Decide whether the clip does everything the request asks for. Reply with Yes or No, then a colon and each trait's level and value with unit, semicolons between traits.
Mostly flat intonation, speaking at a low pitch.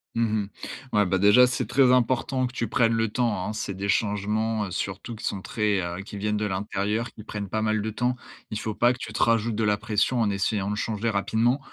Yes: narrow, 2.2 semitones; low, 110 Hz